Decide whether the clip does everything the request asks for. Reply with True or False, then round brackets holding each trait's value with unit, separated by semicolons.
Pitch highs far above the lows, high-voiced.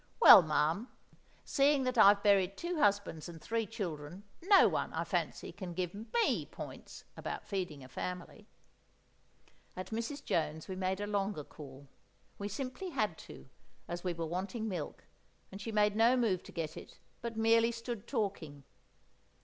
False (4.9 semitones; 200 Hz)